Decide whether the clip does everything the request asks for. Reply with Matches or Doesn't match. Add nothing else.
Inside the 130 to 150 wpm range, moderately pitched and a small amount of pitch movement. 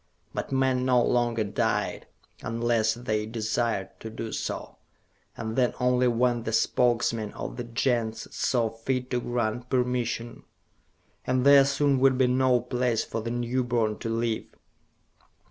Doesn't match